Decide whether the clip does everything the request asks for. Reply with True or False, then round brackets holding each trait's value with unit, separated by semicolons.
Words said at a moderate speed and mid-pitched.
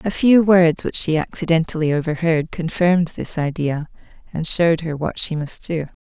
True (170 wpm; 165 Hz)